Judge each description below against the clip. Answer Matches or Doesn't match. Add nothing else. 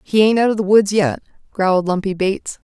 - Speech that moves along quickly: Matches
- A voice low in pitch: Doesn't match